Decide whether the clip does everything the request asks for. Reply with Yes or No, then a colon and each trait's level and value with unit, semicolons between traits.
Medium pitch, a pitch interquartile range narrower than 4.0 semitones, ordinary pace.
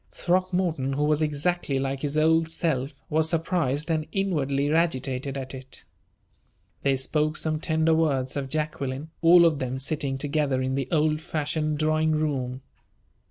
Yes: medium, 150 Hz; average, 2.8 semitones; average, 150 wpm